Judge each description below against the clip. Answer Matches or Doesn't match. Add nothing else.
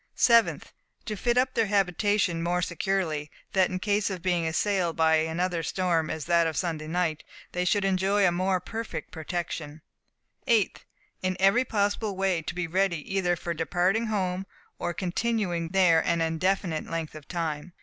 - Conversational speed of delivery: Matches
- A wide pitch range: Doesn't match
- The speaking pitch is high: Doesn't match